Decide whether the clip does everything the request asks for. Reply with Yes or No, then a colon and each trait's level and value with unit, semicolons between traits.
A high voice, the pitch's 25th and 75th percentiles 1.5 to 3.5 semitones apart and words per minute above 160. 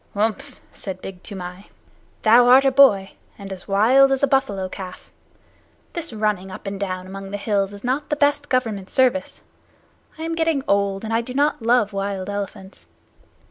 No: high, 210 Hz; average, 5.3 semitones; average, 180 wpm